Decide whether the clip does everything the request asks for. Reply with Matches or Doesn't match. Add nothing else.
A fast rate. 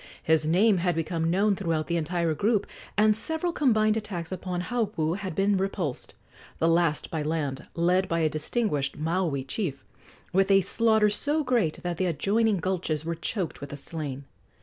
Doesn't match